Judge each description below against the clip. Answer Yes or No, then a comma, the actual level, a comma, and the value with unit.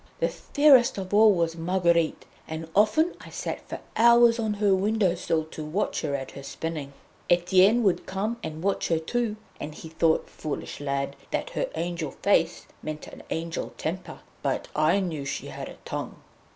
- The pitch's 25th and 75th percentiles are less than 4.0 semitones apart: No, average, 4.8 semitones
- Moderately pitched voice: Yes, medium, 175 Hz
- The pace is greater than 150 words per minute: Yes, average, 180 wpm